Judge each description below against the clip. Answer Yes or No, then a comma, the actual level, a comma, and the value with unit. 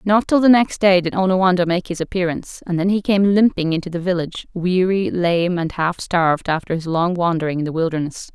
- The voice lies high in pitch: No, medium, 180 Hz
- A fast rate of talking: Yes, fast, 215 wpm